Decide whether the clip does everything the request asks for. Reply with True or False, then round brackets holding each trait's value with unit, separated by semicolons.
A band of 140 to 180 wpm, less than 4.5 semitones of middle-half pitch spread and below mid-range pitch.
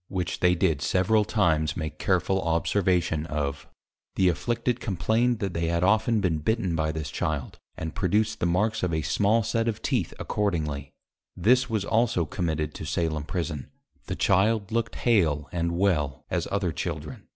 False (165 wpm; 5.2 semitones; 90 Hz)